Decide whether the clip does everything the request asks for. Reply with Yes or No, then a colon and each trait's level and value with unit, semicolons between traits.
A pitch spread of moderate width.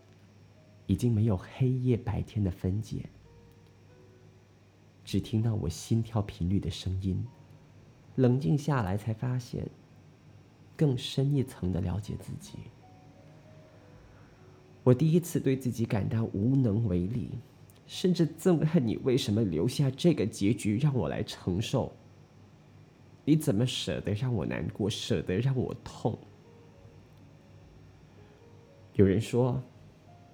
Yes: average, 4.9 semitones